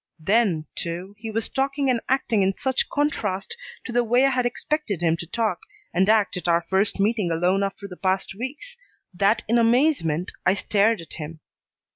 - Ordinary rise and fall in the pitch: Yes, average, 4.7 semitones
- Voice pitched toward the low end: No, high, 210 Hz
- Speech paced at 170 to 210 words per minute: Yes, average, 185 wpm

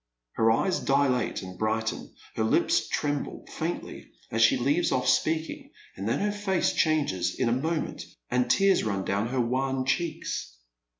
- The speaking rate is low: No, average, 160 wpm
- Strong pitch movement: Yes, wide, 5.8 semitones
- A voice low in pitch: Yes, low, 130 Hz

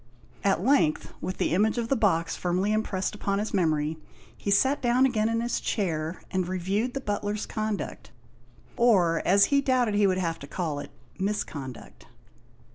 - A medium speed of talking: Yes, average, 170 wpm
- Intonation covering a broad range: No, average, 4.3 semitones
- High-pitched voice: Yes, high, 200 Hz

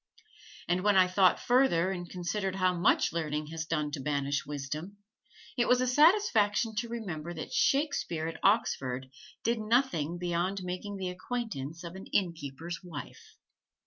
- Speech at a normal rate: Yes, average, 155 wpm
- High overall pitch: No, medium, 180 Hz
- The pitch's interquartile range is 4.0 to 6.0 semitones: Yes, average, 4.9 semitones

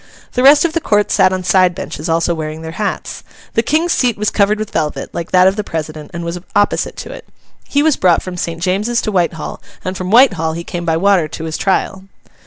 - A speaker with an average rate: No, fast, 230 wpm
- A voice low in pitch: No, medium, 185 Hz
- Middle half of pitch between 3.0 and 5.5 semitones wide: Yes, average, 4.1 semitones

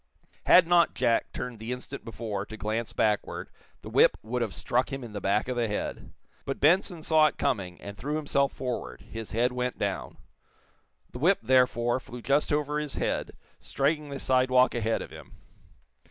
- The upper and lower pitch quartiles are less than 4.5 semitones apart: Yes, average, 3.9 semitones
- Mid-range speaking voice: No, low, 125 Hz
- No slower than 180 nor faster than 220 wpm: Yes, average, 185 wpm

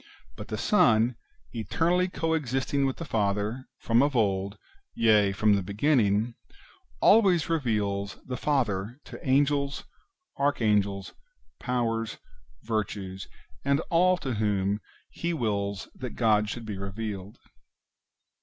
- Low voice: Yes, low, 115 Hz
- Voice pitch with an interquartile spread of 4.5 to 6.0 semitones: Yes, wide, 5.5 semitones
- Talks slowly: Yes, slow, 115 wpm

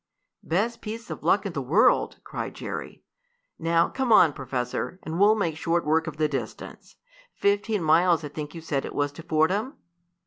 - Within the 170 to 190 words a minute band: Yes, average, 180 wpm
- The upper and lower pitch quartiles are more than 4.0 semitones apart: Yes, average, 4.8 semitones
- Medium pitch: Yes, medium, 165 Hz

